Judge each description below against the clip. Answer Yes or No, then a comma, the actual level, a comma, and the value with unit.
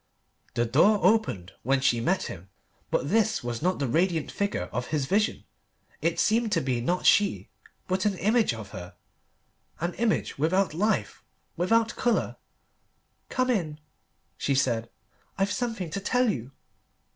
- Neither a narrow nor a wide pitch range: No, wide, 8.3 semitones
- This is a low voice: No, medium, 175 Hz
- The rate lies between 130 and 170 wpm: Yes, average, 150 wpm